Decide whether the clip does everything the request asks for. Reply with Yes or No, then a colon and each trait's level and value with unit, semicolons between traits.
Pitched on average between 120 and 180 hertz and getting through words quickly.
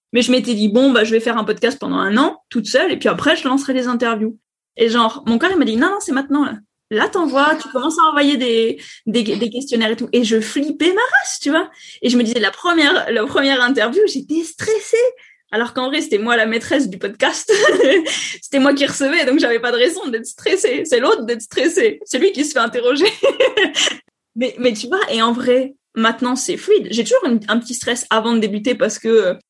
No: very high, 260 Hz; fast, 240 wpm